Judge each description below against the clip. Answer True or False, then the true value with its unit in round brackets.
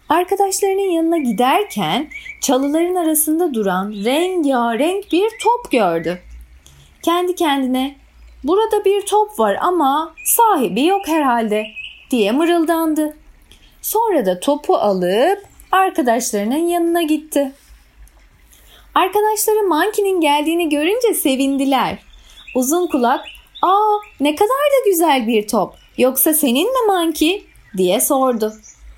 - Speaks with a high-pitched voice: True (310 Hz)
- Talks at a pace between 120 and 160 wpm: False (100 wpm)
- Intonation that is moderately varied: False (6.5 semitones)